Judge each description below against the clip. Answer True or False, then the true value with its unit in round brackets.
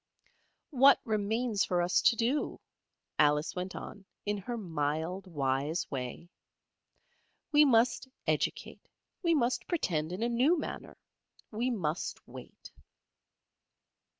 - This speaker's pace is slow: True (115 wpm)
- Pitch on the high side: True (205 Hz)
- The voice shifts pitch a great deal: True (7.0 semitones)